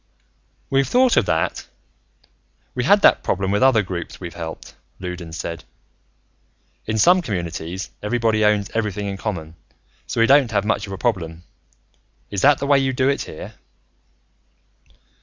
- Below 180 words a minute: Yes, average, 160 wpm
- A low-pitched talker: Yes, low, 105 Hz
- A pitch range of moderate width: No, wide, 6.4 semitones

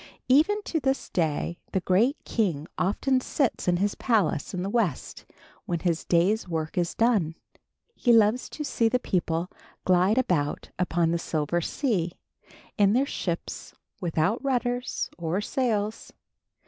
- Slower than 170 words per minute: Yes, average, 145 wpm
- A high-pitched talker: Yes, high, 195 Hz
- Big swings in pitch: Yes, wide, 6.1 semitones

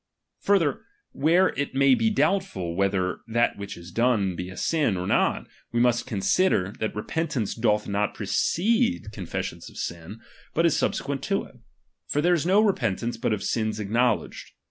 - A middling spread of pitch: No, wide, 8.2 semitones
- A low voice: Yes, low, 120 Hz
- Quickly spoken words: No, average, 170 wpm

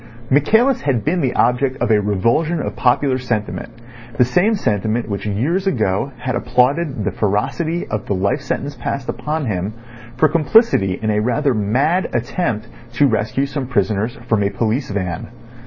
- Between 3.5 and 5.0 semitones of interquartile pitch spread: No, wide, 5.6 semitones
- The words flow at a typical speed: Yes, average, 165 wpm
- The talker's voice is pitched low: Yes, low, 125 Hz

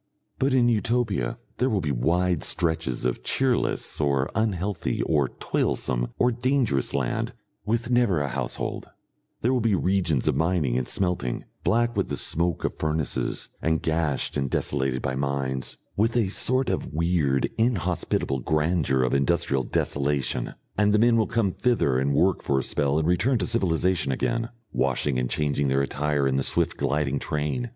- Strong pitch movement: Yes, wide, 7.5 semitones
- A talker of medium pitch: No, very low, 80 Hz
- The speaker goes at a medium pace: Yes, average, 165 wpm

